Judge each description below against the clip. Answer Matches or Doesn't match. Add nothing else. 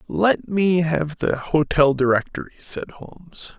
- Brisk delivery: Doesn't match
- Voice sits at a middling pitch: Matches